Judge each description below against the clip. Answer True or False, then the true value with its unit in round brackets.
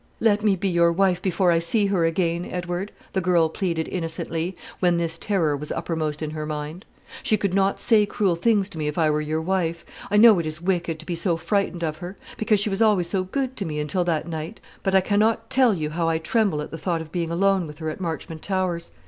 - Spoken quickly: True (240 wpm)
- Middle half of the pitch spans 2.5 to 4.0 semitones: True (3.3 semitones)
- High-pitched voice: False (175 Hz)